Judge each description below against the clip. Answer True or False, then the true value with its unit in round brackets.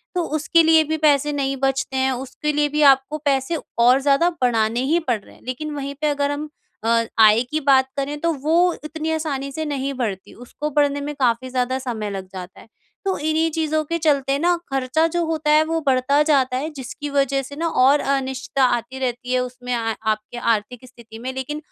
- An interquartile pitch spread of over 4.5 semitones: False (3.1 semitones)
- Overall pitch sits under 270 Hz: False (275 Hz)